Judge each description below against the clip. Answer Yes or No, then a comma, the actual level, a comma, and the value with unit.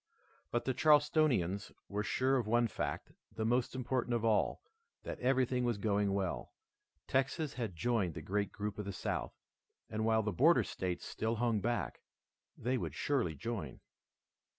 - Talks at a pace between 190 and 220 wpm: No, average, 160 wpm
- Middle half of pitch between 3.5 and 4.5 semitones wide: Yes, average, 3.9 semitones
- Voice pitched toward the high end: No, low, 115 Hz